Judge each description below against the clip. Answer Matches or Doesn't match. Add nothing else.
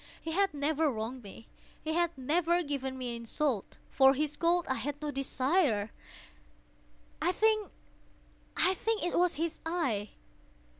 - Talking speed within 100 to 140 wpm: Matches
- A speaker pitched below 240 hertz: Doesn't match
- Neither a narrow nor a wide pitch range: Matches